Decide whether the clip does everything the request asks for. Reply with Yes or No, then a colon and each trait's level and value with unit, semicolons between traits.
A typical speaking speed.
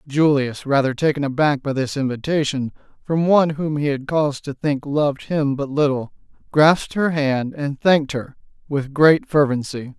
Yes: average, 170 wpm